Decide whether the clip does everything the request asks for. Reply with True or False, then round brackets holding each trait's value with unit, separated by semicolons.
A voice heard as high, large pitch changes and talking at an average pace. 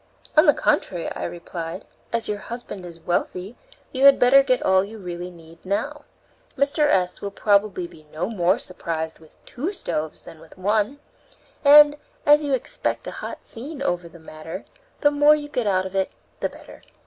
True (200 Hz; 7.9 semitones; 185 wpm)